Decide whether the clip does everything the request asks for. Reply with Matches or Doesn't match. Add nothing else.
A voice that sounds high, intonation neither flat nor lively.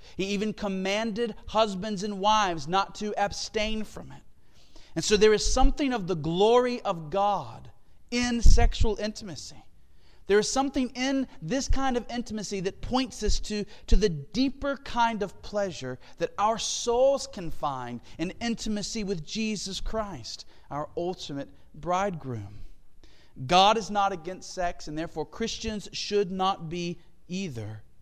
Matches